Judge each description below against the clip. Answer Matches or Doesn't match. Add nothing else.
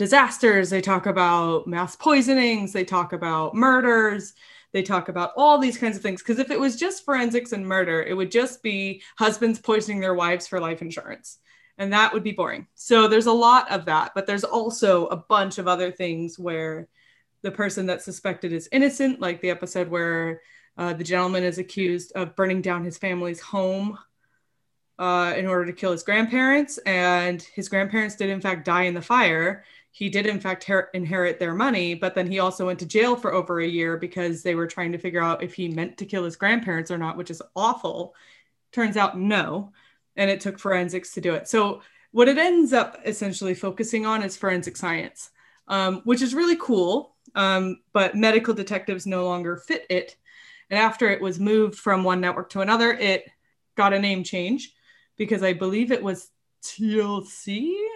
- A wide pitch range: Doesn't match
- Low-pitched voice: Doesn't match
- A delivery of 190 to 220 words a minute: Matches